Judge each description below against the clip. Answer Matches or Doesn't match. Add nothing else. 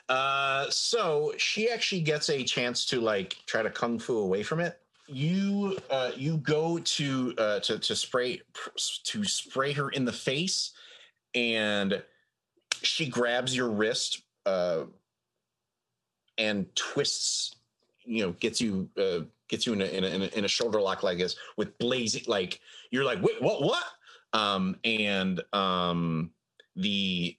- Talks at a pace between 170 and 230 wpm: Doesn't match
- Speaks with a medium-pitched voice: Doesn't match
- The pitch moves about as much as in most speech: Doesn't match